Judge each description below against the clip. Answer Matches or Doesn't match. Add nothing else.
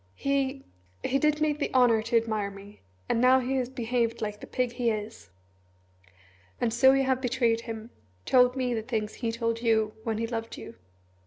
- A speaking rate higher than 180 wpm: Matches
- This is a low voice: Doesn't match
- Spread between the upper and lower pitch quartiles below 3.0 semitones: Matches